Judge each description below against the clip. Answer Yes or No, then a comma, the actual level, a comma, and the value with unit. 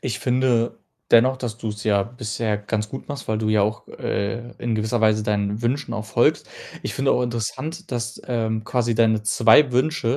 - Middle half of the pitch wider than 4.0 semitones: No, narrow, 2.4 semitones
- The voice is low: Yes, low, 115 Hz